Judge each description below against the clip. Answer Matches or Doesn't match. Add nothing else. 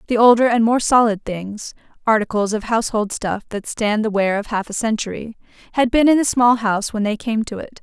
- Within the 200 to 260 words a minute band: Matches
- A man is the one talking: Doesn't match